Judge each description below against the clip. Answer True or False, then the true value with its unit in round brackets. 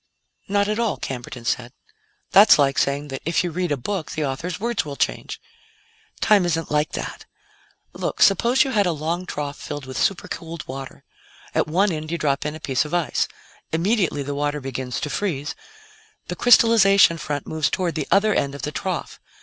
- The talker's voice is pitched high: False (160 Hz)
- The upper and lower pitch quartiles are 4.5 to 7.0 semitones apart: True (5.1 semitones)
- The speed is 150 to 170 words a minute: False (190 wpm)